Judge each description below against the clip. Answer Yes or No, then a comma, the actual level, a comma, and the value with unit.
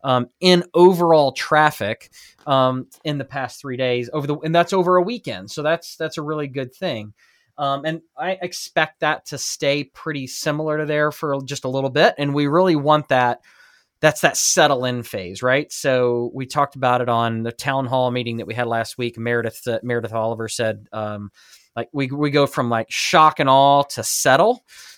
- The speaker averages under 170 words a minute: No, average, 200 wpm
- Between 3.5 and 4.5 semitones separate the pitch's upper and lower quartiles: Yes, average, 4.2 semitones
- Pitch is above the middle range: No, medium, 140 Hz